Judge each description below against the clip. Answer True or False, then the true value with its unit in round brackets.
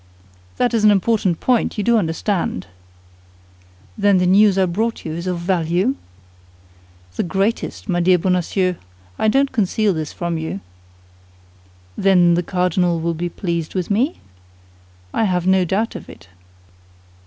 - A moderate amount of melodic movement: True (3.4 semitones)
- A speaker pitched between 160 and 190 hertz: True (185 Hz)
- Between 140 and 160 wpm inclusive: True (145 wpm)